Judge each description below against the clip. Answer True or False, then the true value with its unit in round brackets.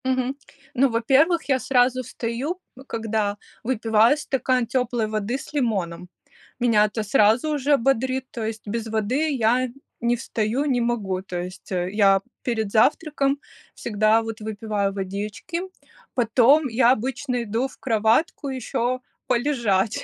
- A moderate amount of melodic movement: True (3.4 semitones)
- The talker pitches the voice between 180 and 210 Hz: False (235 Hz)